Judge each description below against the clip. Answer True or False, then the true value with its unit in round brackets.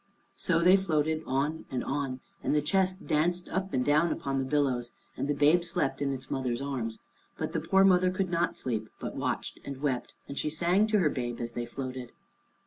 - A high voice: False (145 Hz)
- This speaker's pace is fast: True (210 wpm)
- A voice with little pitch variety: False (5.0 semitones)